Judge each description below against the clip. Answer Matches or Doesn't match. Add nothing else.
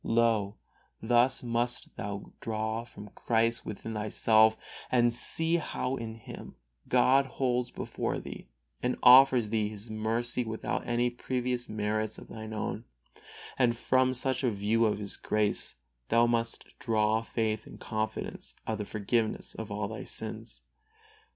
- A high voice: Doesn't match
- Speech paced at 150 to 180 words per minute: Doesn't match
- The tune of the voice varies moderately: Doesn't match